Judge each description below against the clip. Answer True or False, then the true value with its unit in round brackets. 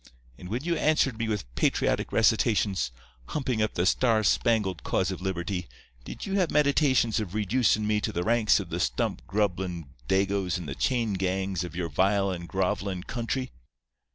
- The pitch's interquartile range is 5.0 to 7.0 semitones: False (4.1 semitones)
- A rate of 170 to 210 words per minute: True (175 wpm)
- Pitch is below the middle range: True (100 Hz)